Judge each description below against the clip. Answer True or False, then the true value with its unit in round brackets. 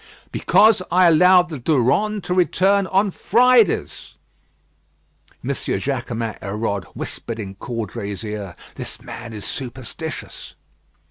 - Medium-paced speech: False (110 wpm)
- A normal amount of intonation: False (8.9 semitones)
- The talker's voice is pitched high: False (135 Hz)